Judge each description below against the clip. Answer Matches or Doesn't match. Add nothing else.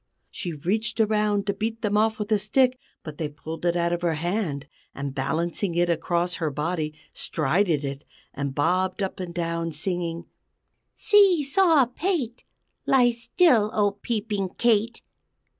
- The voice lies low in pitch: Doesn't match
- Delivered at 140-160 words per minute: Matches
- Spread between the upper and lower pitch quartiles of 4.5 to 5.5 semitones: Matches